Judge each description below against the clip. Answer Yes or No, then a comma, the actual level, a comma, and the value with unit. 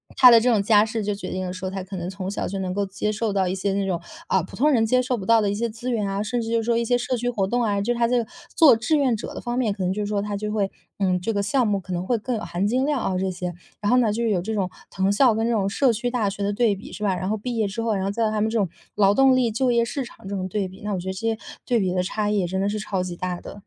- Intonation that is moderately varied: Yes, average, 3.3 semitones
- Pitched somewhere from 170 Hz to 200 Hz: No, high, 210 Hz